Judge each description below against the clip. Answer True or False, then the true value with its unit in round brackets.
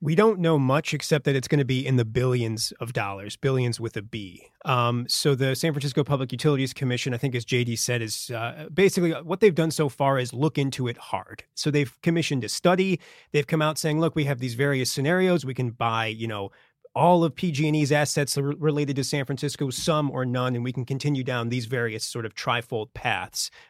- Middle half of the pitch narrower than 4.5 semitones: True (3.9 semitones)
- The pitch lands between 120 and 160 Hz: True (140 Hz)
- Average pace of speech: False (225 wpm)